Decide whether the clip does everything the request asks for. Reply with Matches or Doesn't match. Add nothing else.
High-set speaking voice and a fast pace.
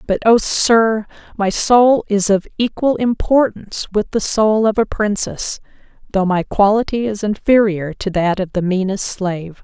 Doesn't match